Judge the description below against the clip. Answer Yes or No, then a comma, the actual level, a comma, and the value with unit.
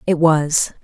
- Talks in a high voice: No, medium, 160 Hz